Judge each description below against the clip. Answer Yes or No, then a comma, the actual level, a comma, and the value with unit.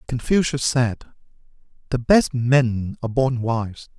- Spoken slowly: Yes, slow, 120 wpm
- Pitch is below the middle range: Yes, low, 125 Hz